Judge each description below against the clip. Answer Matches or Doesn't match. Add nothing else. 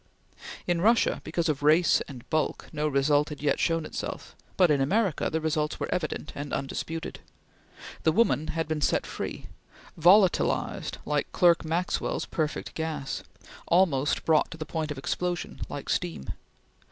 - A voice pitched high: Doesn't match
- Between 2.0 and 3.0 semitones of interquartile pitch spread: Matches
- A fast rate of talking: Doesn't match